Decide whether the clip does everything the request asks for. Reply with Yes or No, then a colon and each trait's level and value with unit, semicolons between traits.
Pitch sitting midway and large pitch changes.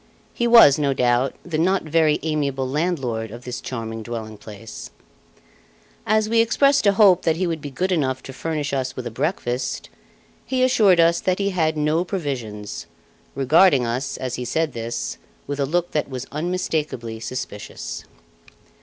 Yes: medium, 145 Hz; wide, 6.0 semitones